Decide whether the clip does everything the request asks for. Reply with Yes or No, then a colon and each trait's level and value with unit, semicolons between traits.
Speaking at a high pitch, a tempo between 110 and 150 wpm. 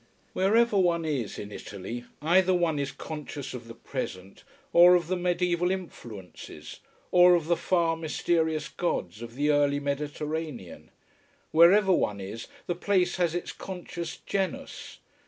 No: medium, 165 Hz; average, 140 wpm